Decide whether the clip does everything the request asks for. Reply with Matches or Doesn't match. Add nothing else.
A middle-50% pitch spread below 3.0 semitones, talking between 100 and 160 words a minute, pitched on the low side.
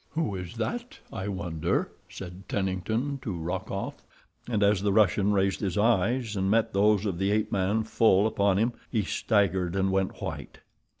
Doesn't match